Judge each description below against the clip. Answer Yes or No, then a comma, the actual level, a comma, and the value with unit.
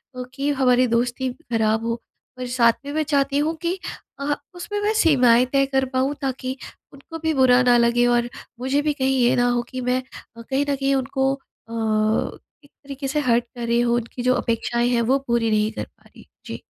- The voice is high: Yes, very high, 255 Hz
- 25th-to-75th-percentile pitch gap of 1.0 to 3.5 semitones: Yes, narrow, 2.6 semitones